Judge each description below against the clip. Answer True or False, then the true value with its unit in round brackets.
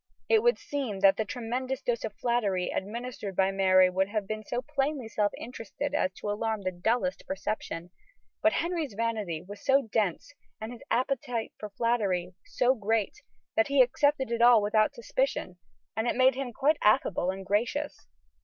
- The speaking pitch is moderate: False (225 Hz)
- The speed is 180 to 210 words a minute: False (170 wpm)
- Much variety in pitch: False (4.5 semitones)